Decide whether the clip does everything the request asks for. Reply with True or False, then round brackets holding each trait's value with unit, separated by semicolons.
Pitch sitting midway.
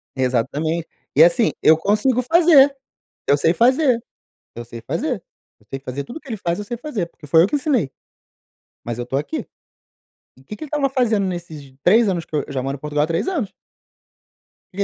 True (175 Hz)